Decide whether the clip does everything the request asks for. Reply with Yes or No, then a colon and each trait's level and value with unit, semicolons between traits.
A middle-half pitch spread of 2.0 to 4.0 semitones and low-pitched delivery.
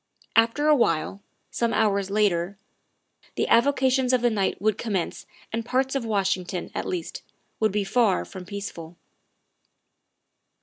No: average, 3.7 semitones; high, 210 Hz